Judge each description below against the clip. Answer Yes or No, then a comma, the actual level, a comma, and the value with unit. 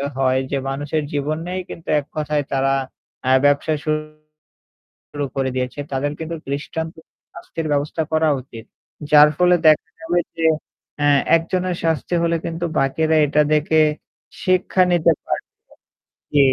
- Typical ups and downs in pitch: No, narrow, 2.3 semitones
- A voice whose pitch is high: No, medium, 155 Hz